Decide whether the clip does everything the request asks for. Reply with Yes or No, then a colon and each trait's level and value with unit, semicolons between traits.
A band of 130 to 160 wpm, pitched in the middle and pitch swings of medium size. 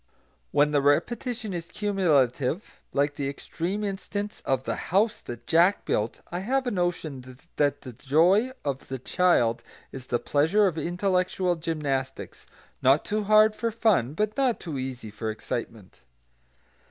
No: average, 150 wpm; medium, 165 Hz; wide, 7.3 semitones